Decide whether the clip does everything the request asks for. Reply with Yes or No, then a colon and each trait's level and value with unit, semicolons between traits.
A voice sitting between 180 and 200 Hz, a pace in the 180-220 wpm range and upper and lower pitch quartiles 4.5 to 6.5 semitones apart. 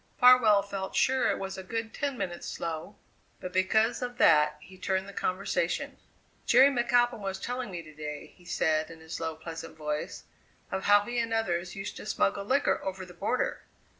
Yes: high, 190 Hz; average, 190 wpm; average, 5.2 semitones